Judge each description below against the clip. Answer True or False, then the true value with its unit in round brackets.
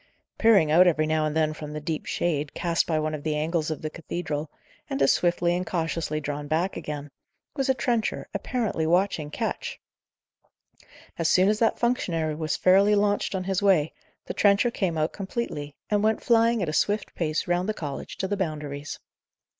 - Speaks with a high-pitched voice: False (170 Hz)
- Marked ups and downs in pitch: False (4.5 semitones)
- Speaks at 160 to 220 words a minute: True (190 wpm)